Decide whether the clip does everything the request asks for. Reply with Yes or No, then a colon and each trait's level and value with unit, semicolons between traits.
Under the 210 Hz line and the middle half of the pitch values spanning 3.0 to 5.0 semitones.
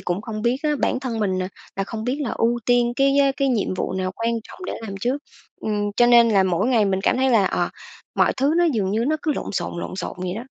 No: high, 230 Hz; average, 4.7 semitones